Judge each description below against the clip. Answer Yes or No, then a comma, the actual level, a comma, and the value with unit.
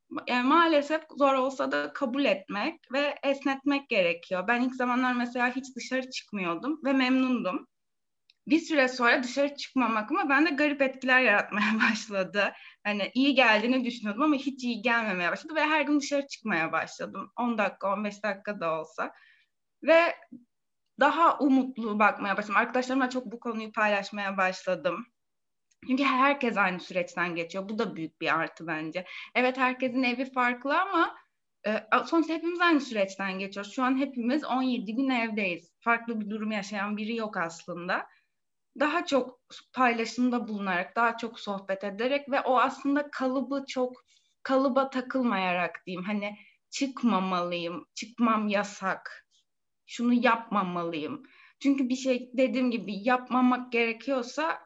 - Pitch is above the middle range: Yes, high, 245 Hz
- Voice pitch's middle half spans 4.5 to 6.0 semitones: Yes, average, 4.9 semitones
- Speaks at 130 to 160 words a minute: Yes, fast, 140 wpm